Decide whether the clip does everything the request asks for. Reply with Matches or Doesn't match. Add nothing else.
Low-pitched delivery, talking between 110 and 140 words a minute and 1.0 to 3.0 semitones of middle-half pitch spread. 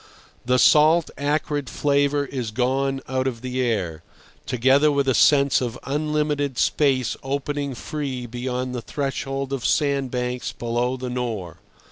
Matches